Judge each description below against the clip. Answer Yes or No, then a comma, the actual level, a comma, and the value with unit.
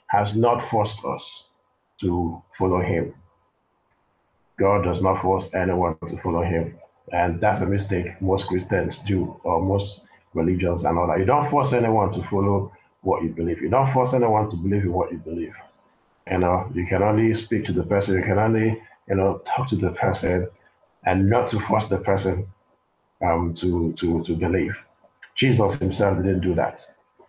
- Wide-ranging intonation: No, average, 2.7 semitones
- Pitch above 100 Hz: No, very low, 95 Hz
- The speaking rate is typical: Yes, average, 180 wpm